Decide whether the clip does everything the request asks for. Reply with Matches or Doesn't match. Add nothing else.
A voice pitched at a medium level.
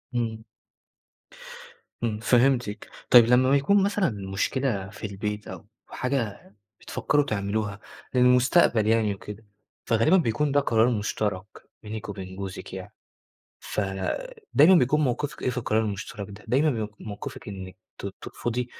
Doesn't match